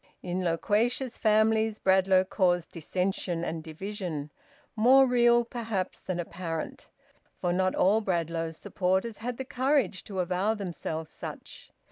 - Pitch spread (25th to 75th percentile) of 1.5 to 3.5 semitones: No, average, 4.2 semitones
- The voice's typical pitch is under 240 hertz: Yes, high, 190 Hz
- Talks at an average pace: No, slow, 125 wpm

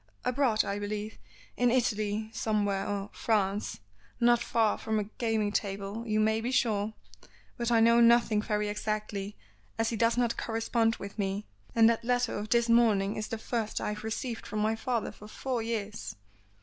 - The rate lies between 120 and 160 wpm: No, average, 175 wpm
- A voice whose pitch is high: Yes, high, 220 Hz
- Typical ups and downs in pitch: No, narrow, 1.9 semitones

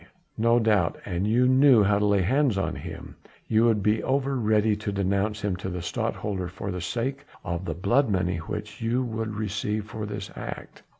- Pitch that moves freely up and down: No, average, 3.0 semitones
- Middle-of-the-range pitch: No, low, 105 Hz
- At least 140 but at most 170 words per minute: No, average, 195 wpm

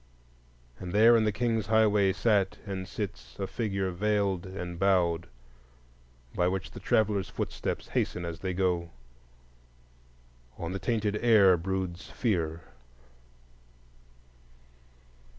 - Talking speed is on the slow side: Yes, slow, 115 wpm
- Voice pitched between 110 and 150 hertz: No, very low, 95 Hz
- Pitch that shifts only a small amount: No, average, 3.0 semitones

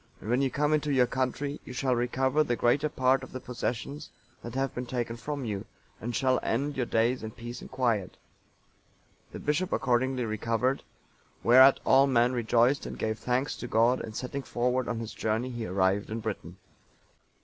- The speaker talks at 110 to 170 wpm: No, average, 190 wpm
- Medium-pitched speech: No, low, 125 Hz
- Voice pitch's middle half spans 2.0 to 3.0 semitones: Yes, narrow, 2.5 semitones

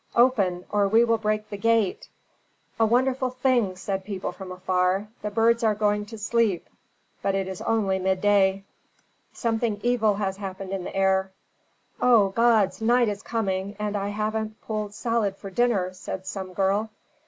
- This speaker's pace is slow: No, average, 165 wpm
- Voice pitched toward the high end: Yes, high, 205 Hz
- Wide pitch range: No, average, 2.8 semitones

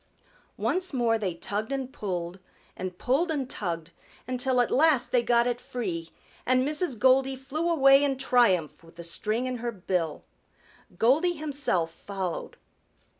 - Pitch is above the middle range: Yes, high, 245 Hz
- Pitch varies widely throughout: Yes, wide, 6.4 semitones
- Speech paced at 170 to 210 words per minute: No, average, 150 wpm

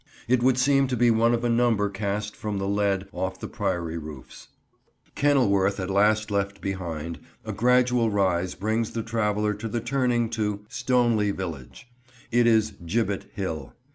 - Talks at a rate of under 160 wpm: No, average, 165 wpm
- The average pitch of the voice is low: Yes, low, 105 Hz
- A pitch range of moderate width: Yes, average, 3.3 semitones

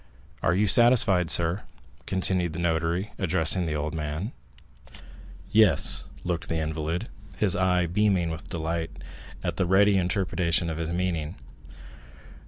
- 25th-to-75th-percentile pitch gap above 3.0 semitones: No, narrow, 2.6 semitones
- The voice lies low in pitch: Yes, very low, 85 Hz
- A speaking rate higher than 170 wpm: No, slow, 135 wpm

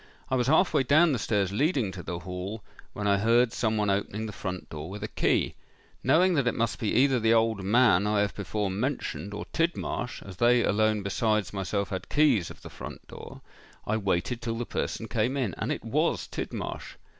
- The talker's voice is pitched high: No, low, 110 Hz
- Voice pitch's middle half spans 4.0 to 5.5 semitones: No, average, 3.6 semitones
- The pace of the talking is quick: Yes, fast, 210 wpm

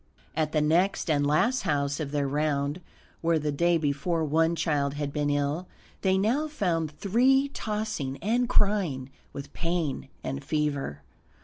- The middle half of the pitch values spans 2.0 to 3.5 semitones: No, average, 4.8 semitones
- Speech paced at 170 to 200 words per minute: No, average, 150 wpm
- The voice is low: No, medium, 155 Hz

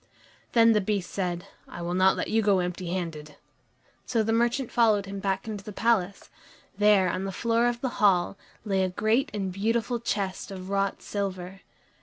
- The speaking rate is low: No, average, 185 wpm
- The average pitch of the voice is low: No, high, 200 Hz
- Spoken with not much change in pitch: No, average, 3.2 semitones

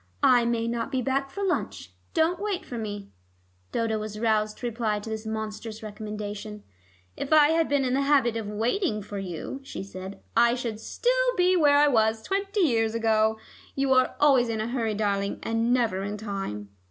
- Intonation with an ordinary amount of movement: Yes, average, 4.3 semitones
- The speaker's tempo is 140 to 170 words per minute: No, average, 190 wpm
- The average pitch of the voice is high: Yes, high, 230 Hz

